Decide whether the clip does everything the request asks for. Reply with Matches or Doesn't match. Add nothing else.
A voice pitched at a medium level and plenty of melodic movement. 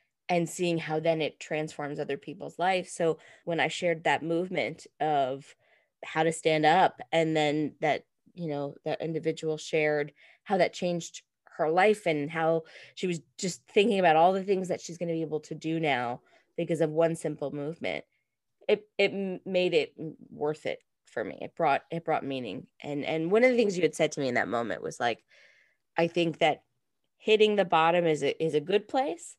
Doesn't match